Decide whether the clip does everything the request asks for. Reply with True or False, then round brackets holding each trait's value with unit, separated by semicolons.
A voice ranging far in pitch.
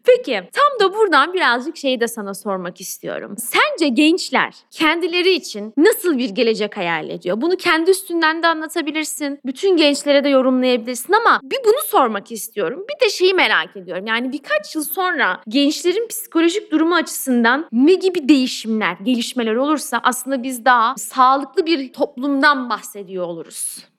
True (6.0 semitones)